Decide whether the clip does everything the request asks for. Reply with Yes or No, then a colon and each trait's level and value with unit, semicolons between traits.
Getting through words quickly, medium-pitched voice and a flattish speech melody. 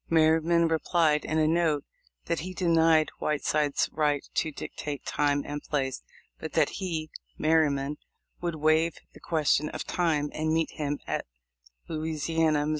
No: average, 150 wpm; medium, 155 Hz; narrow, 1.7 semitones